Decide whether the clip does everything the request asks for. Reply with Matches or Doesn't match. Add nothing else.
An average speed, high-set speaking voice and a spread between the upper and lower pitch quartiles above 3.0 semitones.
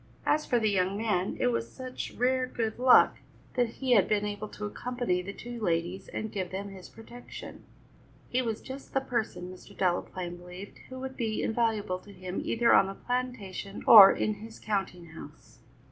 Matches